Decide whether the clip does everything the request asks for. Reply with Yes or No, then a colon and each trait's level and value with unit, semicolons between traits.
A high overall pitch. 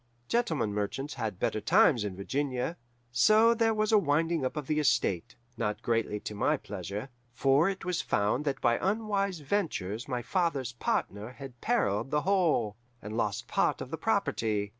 No: low, 135 Hz